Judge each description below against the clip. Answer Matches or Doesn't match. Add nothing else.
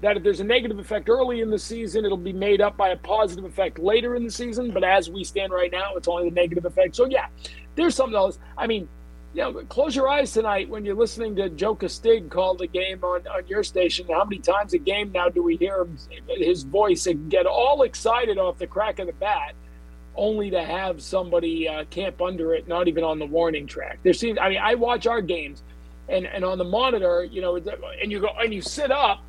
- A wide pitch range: Doesn't match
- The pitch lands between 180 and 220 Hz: Matches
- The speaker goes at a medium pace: Doesn't match